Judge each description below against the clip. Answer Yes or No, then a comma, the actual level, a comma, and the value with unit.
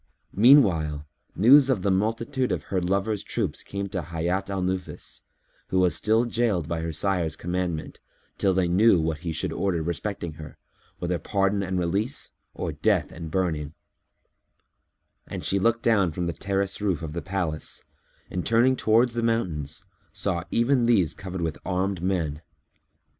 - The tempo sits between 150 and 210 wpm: Yes, average, 160 wpm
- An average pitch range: Yes, average, 3.9 semitones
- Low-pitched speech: Yes, very low, 95 Hz